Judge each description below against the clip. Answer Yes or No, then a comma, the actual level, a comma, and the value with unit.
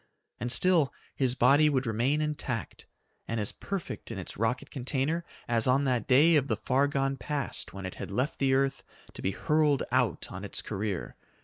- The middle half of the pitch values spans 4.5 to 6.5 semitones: No, average, 3.8 semitones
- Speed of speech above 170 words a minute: Yes, average, 190 wpm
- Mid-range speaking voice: No, low, 130 Hz